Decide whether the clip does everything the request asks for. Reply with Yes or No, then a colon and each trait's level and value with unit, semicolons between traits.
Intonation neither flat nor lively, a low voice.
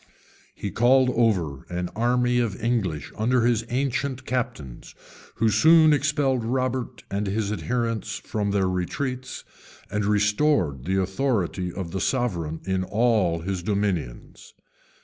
Yes: average, 5.0 semitones; low, 110 Hz